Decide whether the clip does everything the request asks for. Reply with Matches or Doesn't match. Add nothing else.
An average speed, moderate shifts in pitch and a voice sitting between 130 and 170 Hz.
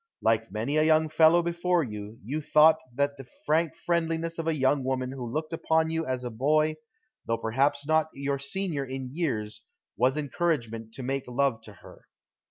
Matches